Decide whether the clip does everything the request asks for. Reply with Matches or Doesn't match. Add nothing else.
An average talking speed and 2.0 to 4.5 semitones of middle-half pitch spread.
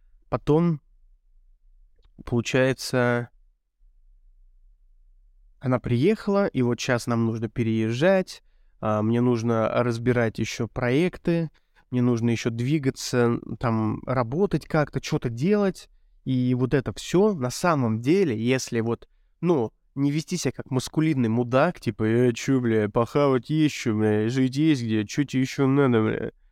Matches